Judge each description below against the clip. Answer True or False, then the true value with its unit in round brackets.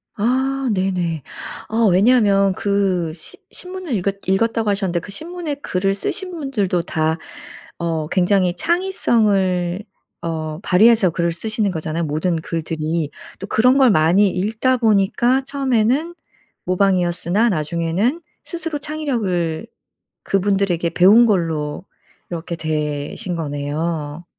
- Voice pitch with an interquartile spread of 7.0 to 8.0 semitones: False (5.5 semitones)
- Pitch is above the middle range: True (195 Hz)